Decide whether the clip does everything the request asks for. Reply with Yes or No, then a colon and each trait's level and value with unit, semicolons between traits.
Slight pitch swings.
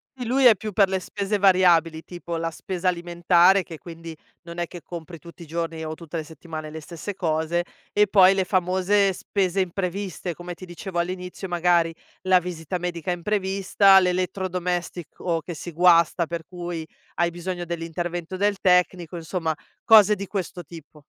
Yes: narrow, 2.0 semitones